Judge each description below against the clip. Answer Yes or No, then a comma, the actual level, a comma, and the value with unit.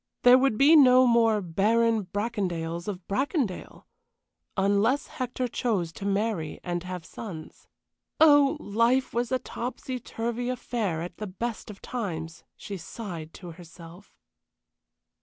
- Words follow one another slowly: Yes, slow, 130 wpm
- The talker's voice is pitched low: No, high, 215 Hz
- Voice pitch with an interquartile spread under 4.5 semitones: No, wide, 5.5 semitones